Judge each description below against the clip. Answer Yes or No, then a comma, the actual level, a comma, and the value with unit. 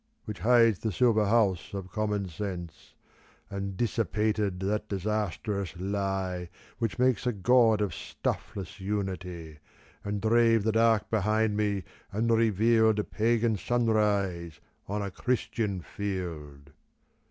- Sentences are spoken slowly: Yes, slow, 120 wpm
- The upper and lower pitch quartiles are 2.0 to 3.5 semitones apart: Yes, average, 2.8 semitones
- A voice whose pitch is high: No, low, 105 Hz